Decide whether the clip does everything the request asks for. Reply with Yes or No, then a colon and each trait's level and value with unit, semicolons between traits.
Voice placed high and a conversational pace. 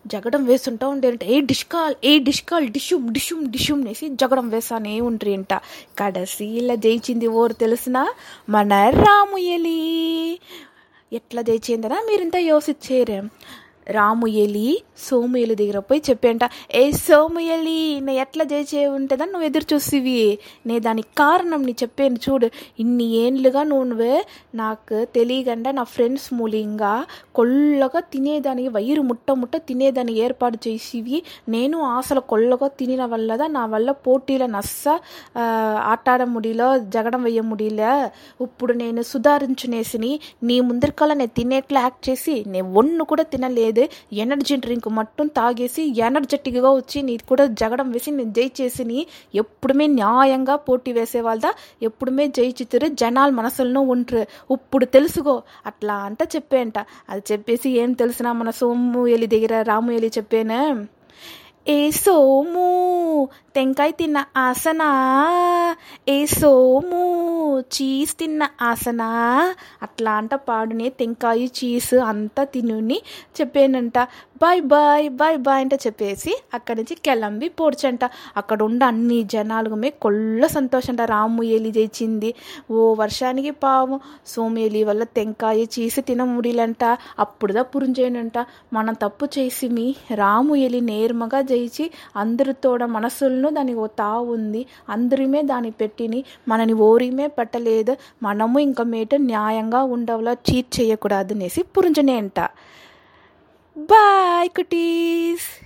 Yes: very high, 255 Hz; average, 105 wpm